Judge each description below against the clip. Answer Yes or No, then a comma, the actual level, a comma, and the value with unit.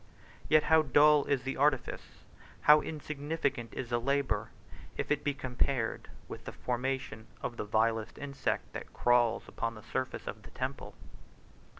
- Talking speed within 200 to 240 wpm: No, average, 155 wpm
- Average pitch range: Yes, average, 3.7 semitones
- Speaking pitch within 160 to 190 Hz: No, low, 130 Hz